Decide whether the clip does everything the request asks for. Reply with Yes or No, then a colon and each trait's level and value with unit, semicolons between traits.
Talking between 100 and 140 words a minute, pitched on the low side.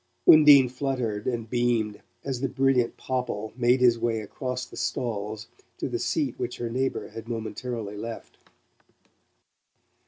Yes: slow, 135 wpm; low, 120 Hz